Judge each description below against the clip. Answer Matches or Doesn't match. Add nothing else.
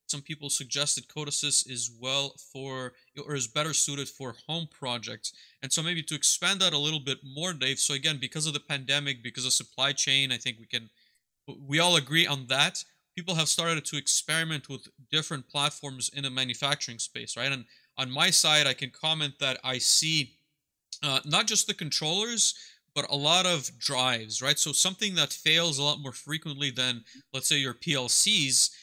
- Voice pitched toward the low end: Doesn't match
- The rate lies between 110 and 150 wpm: Doesn't match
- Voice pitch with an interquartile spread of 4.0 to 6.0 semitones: Doesn't match